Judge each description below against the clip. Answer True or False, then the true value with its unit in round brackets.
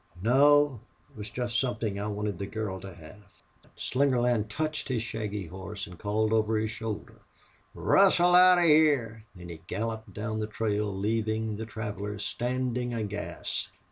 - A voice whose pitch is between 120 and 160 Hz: False (110 Hz)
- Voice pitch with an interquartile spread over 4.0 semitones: False (2.9 semitones)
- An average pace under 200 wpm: True (155 wpm)